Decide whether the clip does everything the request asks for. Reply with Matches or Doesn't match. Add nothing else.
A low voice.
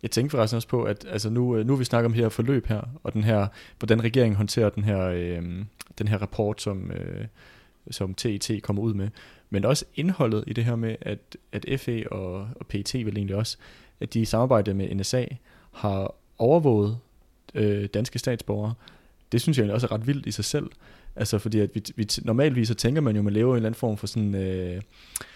Matches